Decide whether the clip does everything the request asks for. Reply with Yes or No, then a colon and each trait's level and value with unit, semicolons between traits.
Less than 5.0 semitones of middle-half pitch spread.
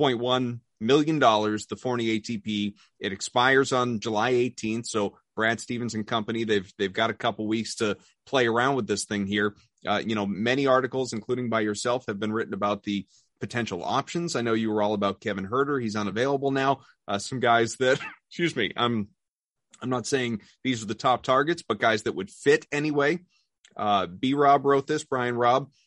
Yes: average, 3.5 semitones